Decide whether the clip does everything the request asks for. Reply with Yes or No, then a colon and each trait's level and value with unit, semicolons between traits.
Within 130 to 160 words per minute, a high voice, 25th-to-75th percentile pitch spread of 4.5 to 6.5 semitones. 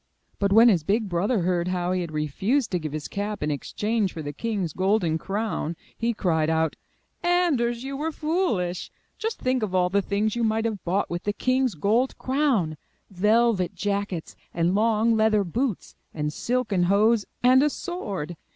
No: average, 180 wpm; high, 205 Hz; average, 5.1 semitones